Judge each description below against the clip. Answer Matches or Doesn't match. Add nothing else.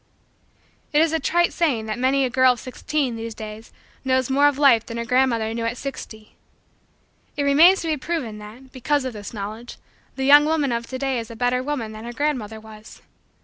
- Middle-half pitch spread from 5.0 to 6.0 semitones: Doesn't match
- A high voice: Matches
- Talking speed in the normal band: Doesn't match